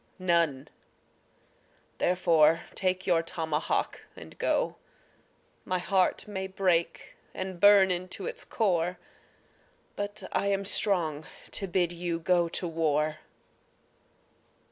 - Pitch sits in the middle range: Yes, medium, 180 Hz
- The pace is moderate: No, slow, 105 wpm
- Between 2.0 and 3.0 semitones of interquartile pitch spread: Yes, narrow, 2.4 semitones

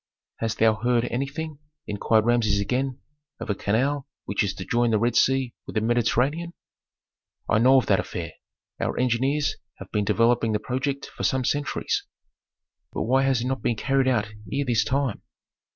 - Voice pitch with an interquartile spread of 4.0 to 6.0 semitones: No, average, 3.5 semitones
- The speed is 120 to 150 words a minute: No, average, 175 wpm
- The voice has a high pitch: No, low, 120 Hz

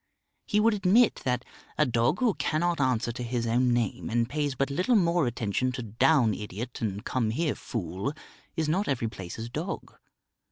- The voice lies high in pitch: No, low, 125 Hz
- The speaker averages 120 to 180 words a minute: Yes, average, 175 wpm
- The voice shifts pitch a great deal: Yes, wide, 5.8 semitones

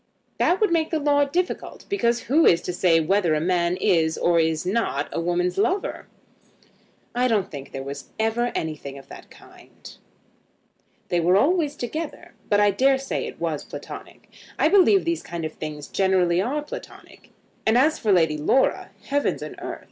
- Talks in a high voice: Yes, high, 200 Hz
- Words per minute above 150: Yes, average, 180 wpm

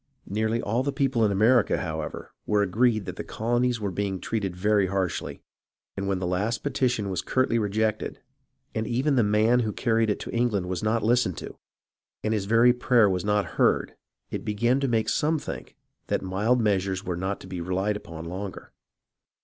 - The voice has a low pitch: Yes, low, 105 Hz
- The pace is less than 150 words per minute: No, average, 190 wpm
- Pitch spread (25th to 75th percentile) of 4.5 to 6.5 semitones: No, average, 3.5 semitones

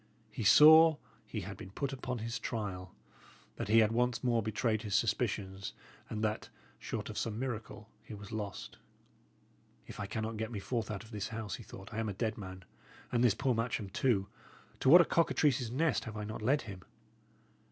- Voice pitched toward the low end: Yes, low, 110 Hz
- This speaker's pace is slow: No, average, 195 wpm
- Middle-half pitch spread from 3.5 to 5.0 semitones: No, average, 2.8 semitones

